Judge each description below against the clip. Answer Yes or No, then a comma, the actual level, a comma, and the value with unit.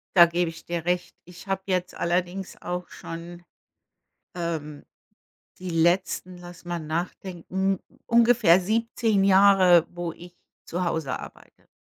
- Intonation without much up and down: Yes, narrow, 1.8 semitones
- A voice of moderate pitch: Yes, medium, 175 Hz